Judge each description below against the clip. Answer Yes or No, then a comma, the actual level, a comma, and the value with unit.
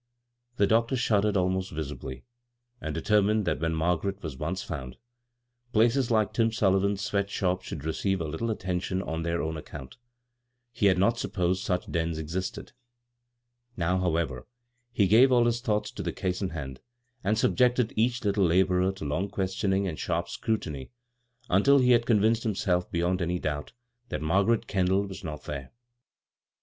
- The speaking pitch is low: Yes, very low, 95 Hz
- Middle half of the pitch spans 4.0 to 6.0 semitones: Yes, average, 4.6 semitones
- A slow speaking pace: No, average, 160 wpm